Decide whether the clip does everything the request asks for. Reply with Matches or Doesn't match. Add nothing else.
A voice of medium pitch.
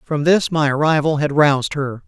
Matches